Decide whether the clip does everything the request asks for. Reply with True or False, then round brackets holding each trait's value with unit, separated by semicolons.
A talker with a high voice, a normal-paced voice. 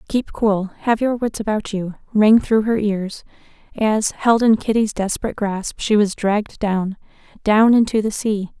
True (210 Hz; 175 wpm)